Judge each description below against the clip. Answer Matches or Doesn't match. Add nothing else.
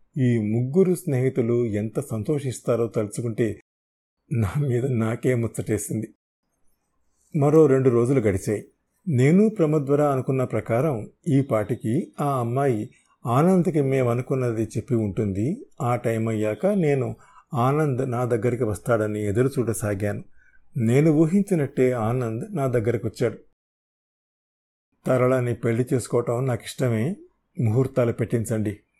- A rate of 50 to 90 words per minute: Doesn't match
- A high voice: Doesn't match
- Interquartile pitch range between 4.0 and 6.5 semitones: Doesn't match